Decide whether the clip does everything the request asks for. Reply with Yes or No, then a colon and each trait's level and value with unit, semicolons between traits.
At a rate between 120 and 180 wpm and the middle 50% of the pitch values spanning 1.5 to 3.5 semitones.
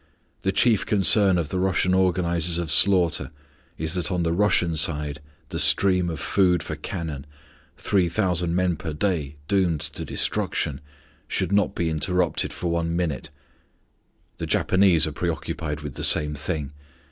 Yes: average, 155 wpm; average, 2.8 semitones